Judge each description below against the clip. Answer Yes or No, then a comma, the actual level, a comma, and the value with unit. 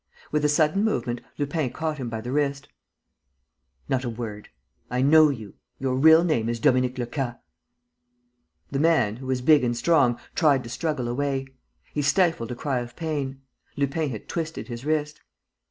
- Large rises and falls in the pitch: No, average, 3.8 semitones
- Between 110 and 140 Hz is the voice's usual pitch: Yes, low, 135 Hz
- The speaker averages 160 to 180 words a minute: Yes, average, 170 wpm